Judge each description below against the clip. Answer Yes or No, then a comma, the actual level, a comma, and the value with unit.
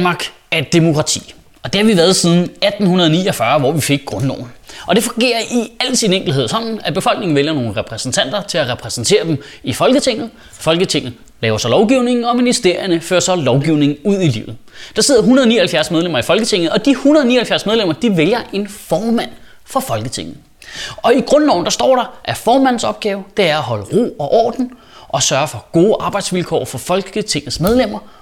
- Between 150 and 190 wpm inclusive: Yes, average, 180 wpm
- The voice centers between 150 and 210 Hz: Yes, high, 190 Hz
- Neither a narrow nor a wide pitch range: No, wide, 6.9 semitones